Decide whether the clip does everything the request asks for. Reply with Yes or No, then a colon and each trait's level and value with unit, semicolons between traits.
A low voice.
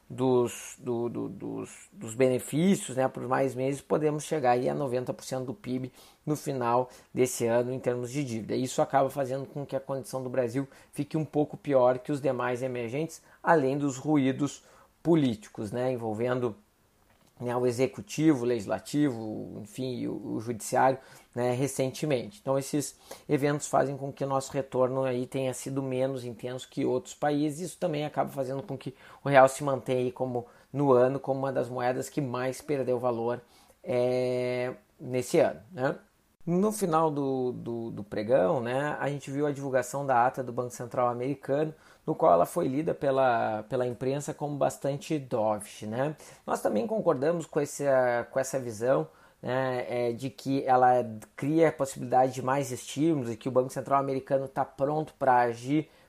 Yes: low, 130 Hz